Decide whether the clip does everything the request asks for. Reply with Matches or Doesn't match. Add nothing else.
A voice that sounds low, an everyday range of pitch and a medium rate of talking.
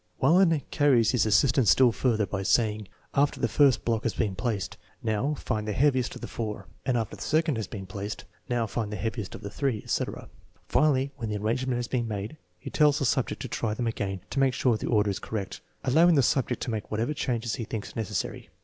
Doesn't match